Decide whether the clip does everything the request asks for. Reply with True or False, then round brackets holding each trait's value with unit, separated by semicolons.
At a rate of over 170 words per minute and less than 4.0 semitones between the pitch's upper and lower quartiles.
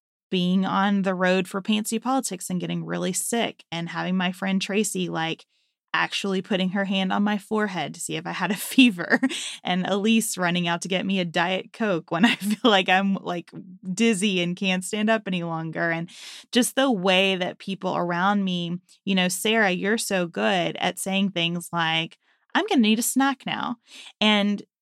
True (195 wpm; 3.1 semitones)